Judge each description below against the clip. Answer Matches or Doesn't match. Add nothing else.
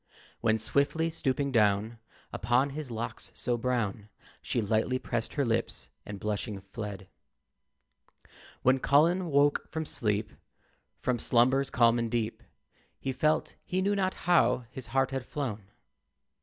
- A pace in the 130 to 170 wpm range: Matches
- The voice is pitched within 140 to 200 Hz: Doesn't match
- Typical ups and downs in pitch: Matches